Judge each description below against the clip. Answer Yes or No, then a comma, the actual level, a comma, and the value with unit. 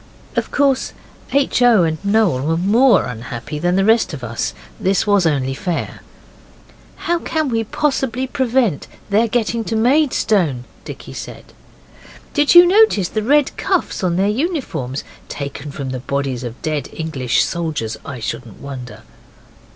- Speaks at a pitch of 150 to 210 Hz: Yes, high, 190 Hz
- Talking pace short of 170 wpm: Yes, average, 150 wpm